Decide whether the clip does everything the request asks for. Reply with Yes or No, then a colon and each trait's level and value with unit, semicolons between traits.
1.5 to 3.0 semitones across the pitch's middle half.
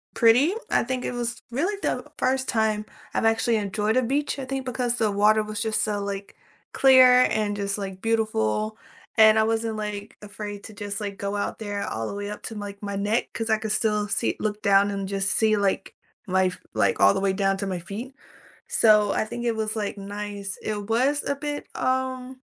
Yes: narrow, 2.5 semitones